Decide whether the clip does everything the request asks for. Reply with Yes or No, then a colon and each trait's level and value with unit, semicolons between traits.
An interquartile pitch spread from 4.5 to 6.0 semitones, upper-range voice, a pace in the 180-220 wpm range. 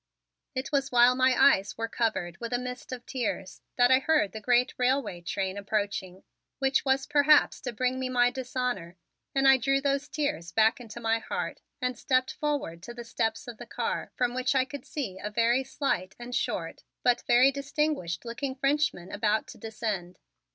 No: average, 3.6 semitones; high, 245 Hz; average, 185 wpm